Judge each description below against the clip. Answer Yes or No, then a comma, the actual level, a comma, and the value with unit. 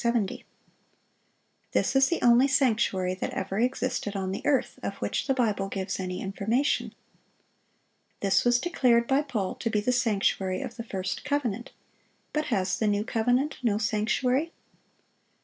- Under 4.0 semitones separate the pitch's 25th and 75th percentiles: No, average, 4.4 semitones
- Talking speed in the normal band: Yes, average, 150 wpm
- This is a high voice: Yes, high, 230 Hz